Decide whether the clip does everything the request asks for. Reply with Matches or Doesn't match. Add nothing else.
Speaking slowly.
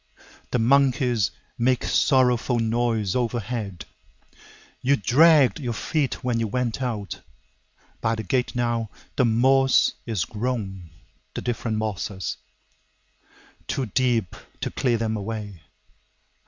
Matches